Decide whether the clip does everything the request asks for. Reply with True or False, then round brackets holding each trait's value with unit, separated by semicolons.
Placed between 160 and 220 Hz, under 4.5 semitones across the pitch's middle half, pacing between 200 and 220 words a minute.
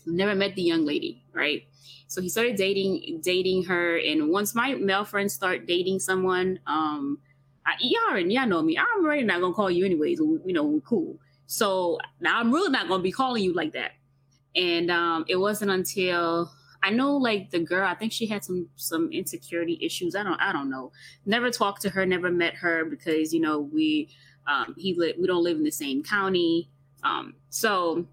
False (185 Hz; 5.6 semitones; 205 wpm)